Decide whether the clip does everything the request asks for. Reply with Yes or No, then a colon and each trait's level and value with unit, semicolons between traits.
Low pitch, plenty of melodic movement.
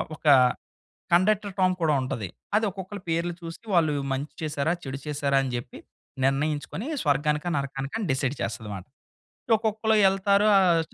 No: medium, 155 Hz; wide, 5.7 semitones